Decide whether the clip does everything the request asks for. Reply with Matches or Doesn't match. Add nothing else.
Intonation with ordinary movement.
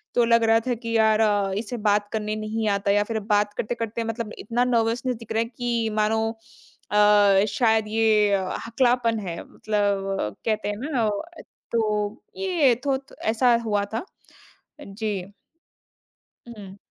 Doesn't match